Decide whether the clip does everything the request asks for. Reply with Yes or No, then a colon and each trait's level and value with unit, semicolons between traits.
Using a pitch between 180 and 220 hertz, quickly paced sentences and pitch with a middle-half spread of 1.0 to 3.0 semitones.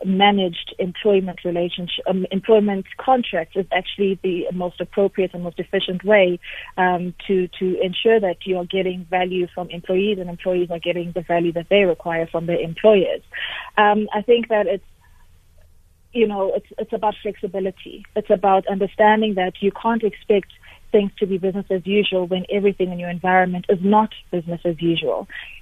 No: medium, 185 Hz; average, 165 wpm; narrow, 2.5 semitones